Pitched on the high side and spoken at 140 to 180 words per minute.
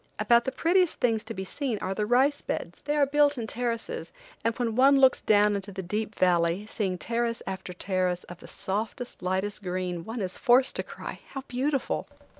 No: high, 220 Hz; average, 200 wpm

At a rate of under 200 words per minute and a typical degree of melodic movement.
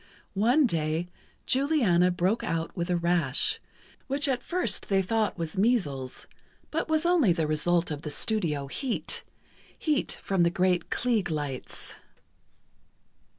No: slow, 135 wpm; wide, 7.0 semitones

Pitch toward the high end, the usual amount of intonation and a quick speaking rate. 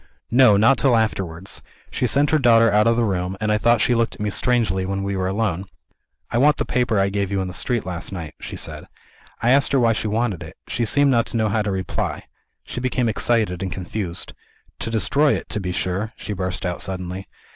No: low, 105 Hz; average, 3.9 semitones; fast, 235 wpm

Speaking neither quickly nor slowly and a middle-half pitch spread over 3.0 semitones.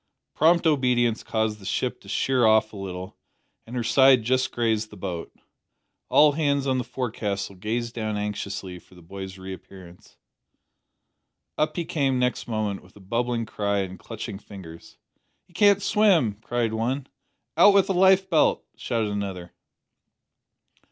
Yes: average, 150 wpm; average, 5.2 semitones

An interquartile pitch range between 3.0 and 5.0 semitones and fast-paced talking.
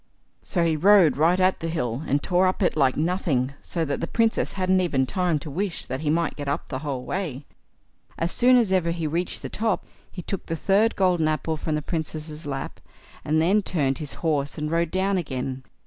Yes: average, 4.0 semitones; fast, 215 wpm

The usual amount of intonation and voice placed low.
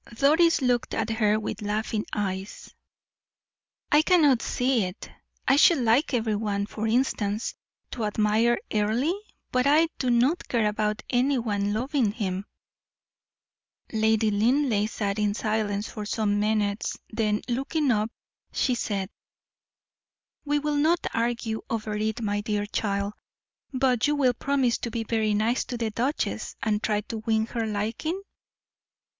No: average, 3.3 semitones; high, 225 Hz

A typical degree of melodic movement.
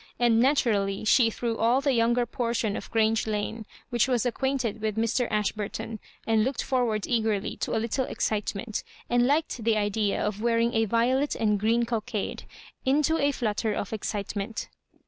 No: narrow, 2.3 semitones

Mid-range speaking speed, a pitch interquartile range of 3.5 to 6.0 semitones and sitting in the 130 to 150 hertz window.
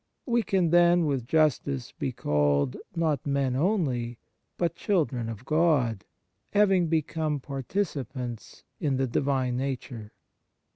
No: slow, 115 wpm; average, 5.3 semitones; medium, 140 Hz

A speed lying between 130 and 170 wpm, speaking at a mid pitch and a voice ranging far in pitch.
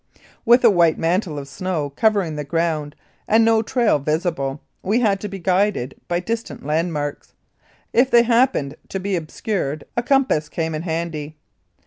Yes: average, 160 wpm; medium, 175 Hz; wide, 6.2 semitones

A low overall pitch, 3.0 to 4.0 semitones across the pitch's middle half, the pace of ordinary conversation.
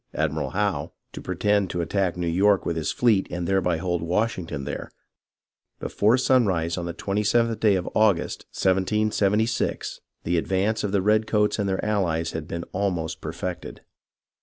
Yes: very low, 95 Hz; average, 3.7 semitones; average, 160 wpm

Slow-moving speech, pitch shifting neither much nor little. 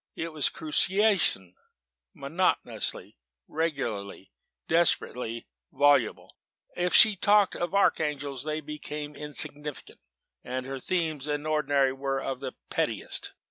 Yes: slow, 110 wpm; average, 3.3 semitones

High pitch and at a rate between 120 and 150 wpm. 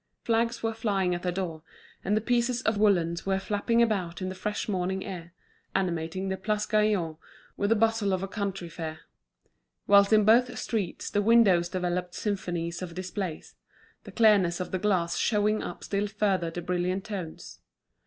No: high, 195 Hz; average, 170 wpm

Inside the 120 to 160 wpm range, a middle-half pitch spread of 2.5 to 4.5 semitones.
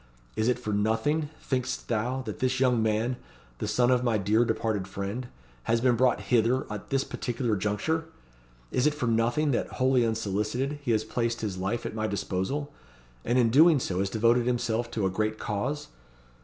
No: average, 185 wpm; average, 3.1 semitones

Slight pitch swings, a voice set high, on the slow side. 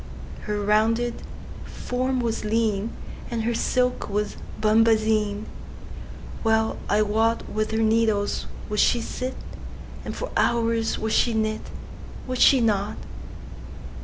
Yes: narrow, 1.5 semitones; high, 220 Hz; slow, 100 wpm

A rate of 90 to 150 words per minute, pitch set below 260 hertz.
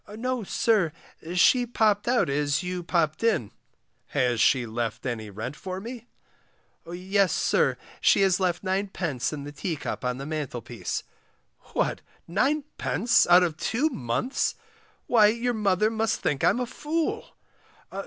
Yes: average, 140 wpm; medium, 185 Hz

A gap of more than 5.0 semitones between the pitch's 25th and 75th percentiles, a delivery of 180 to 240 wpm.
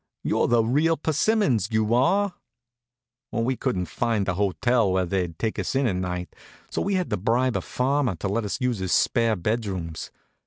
Yes: wide, 5.5 semitones; average, 190 wpm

